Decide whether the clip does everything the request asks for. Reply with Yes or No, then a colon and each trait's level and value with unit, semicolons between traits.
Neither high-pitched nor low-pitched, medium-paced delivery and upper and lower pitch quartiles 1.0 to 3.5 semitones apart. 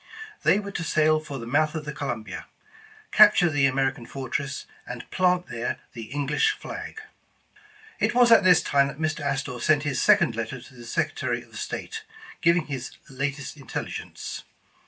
No: medium, 145 Hz; average, 170 wpm; average, 4.0 semitones